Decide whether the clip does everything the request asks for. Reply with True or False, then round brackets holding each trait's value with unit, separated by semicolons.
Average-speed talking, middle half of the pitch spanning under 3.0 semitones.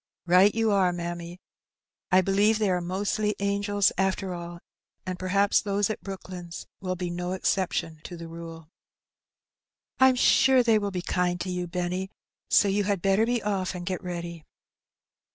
True (165 wpm; 2.4 semitones)